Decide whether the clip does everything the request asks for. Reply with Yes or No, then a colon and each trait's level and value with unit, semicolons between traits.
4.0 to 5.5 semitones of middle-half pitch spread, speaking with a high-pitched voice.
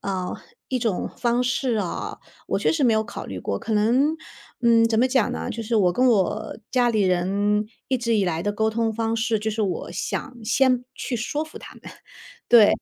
No: average, 2.9 semitones; high, 225 Hz